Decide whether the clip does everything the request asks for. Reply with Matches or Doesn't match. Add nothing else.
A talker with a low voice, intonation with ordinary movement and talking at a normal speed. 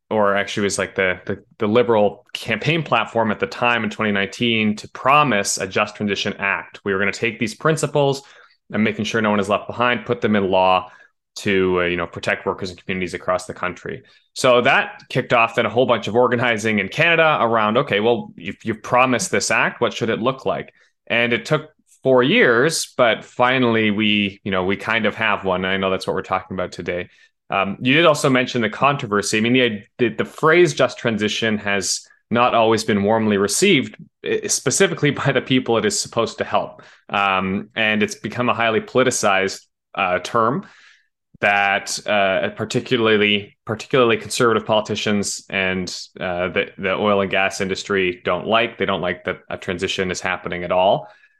Matches